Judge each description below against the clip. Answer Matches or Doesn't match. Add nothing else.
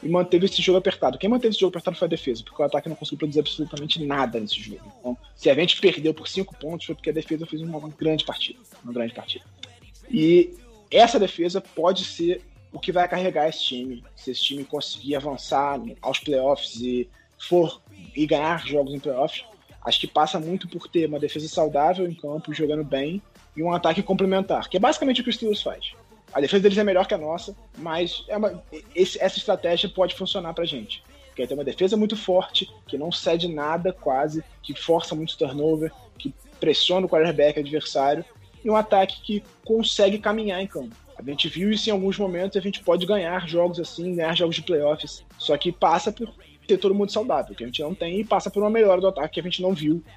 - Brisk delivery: Matches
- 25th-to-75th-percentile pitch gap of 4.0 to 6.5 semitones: Matches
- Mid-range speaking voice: Matches